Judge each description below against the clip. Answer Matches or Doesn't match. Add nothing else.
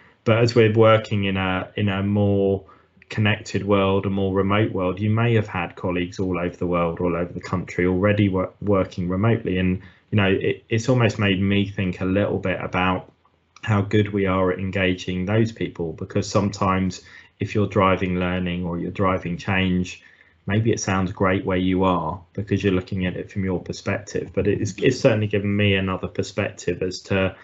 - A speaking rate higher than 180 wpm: Matches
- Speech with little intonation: Matches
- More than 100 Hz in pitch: Doesn't match